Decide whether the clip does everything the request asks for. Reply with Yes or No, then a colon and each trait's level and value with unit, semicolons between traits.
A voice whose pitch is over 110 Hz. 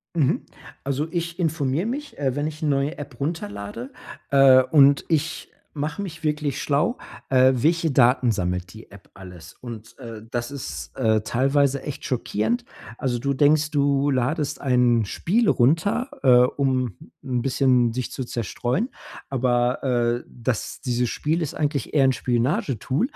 Yes: low, 135 Hz